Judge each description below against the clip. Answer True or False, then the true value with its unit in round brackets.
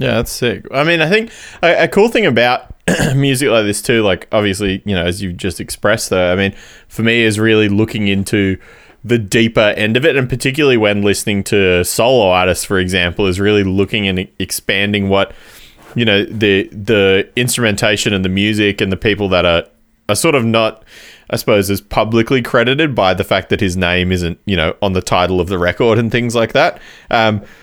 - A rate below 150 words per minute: False (205 wpm)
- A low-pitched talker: True (105 Hz)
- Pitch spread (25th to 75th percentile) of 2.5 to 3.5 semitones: True (2.9 semitones)